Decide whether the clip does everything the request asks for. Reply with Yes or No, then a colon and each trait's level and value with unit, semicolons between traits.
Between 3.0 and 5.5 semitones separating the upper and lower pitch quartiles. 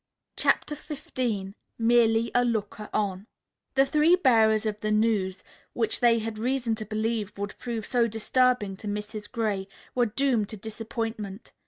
No: narrow, 2.4 semitones